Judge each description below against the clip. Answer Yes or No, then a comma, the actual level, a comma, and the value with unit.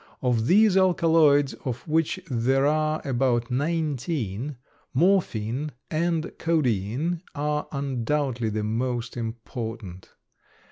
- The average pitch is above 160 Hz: No, low, 135 Hz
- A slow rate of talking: Yes, slow, 95 wpm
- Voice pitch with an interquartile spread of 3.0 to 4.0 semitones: No, average, 5.0 semitones